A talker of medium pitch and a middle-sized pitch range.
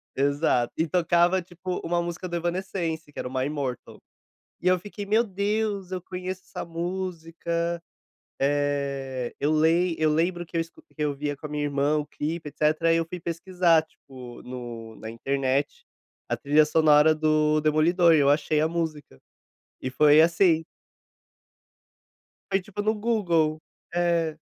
Yes: medium, 160 Hz; average, 3.1 semitones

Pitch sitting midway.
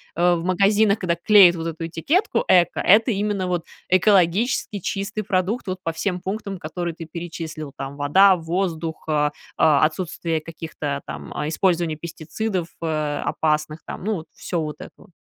Yes: medium, 170 Hz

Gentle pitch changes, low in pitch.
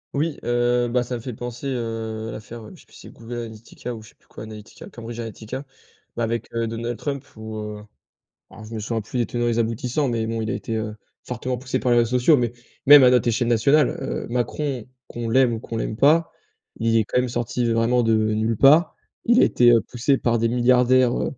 Yes: narrow, 1.8 semitones; low, 120 Hz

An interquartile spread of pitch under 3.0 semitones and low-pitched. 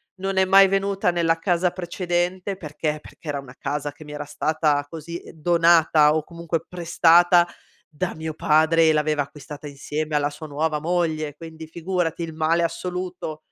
No: narrow, 2.4 semitones; medium, 165 Hz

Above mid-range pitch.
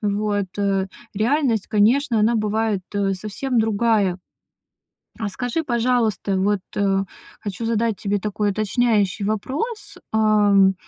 Yes: high, 215 Hz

